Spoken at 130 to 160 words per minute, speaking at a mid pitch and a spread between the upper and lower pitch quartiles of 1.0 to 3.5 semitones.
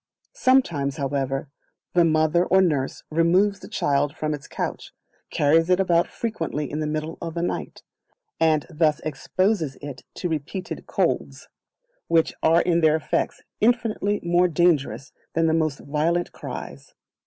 Yes: average, 145 wpm; medium, 165 Hz; average, 2.9 semitones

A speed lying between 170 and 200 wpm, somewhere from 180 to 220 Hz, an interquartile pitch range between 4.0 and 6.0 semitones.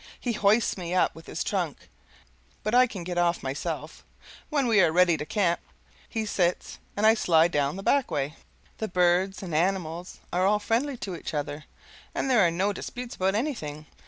Yes: average, 190 wpm; medium, 185 Hz; average, 4.4 semitones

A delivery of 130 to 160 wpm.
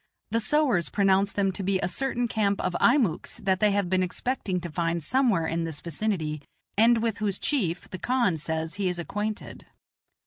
No: average, 185 wpm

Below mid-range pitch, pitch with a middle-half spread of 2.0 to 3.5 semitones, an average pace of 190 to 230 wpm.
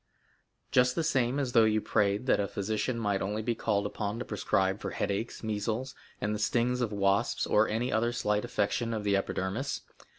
Yes: low, 110 Hz; average, 2.8 semitones; average, 195 wpm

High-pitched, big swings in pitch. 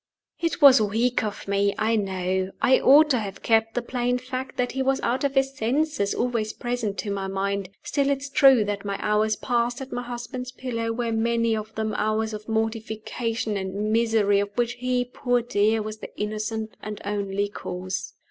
No: high, 225 Hz; average, 3.1 semitones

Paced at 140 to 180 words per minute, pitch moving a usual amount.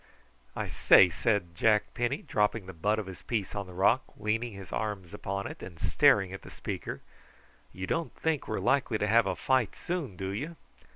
No: fast, 205 wpm; average, 3.6 semitones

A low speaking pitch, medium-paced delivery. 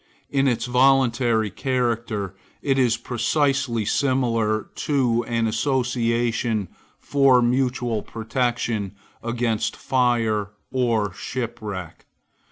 No: low, 120 Hz; slow, 85 wpm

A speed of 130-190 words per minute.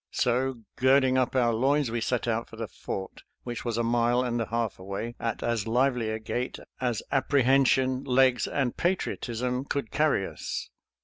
Yes: average, 180 wpm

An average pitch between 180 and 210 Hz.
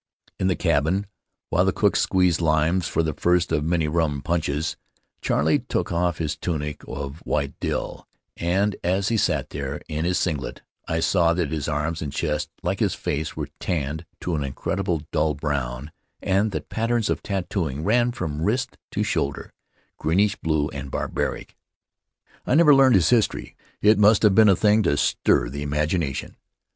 No: very low, 80 Hz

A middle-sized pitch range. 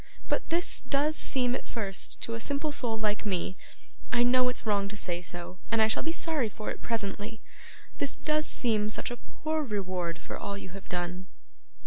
Yes: average, 4.5 semitones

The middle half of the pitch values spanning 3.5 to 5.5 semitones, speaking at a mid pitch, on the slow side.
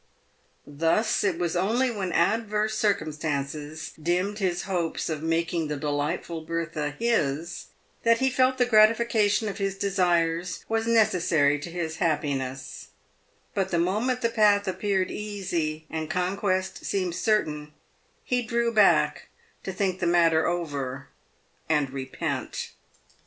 Yes: average, 4.9 semitones; medium, 175 Hz; slow, 130 wpm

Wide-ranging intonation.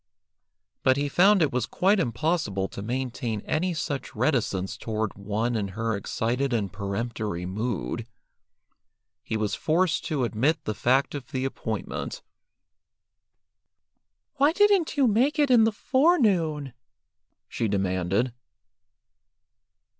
Yes: wide, 8.2 semitones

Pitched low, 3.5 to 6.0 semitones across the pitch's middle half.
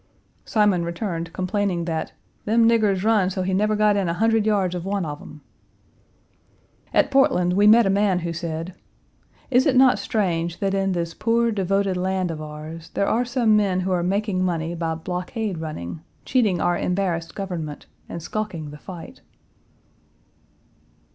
No: medium, 185 Hz; average, 3.8 semitones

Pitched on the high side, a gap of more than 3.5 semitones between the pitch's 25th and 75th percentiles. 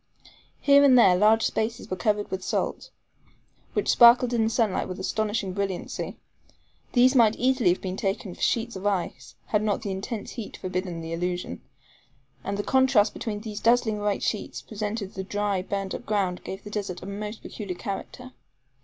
No: high, 205 Hz; average, 3.0 semitones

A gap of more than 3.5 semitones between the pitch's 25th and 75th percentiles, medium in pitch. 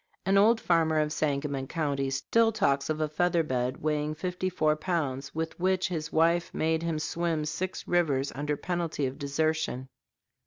No: average, 3.1 semitones; medium, 155 Hz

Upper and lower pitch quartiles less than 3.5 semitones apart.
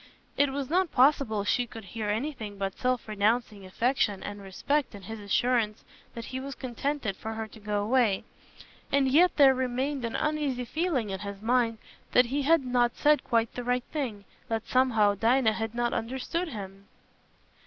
No: average, 4.0 semitones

